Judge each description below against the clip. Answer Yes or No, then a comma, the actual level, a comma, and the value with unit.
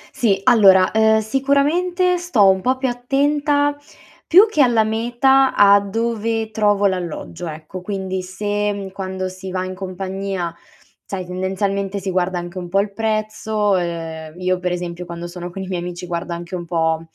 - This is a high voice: Yes, high, 195 Hz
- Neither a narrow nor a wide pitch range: Yes, average, 3.6 semitones